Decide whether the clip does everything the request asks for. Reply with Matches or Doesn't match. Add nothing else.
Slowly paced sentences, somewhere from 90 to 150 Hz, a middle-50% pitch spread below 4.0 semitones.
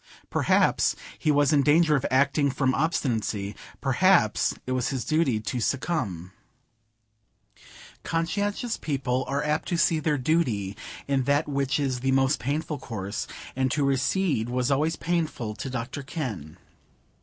Doesn't match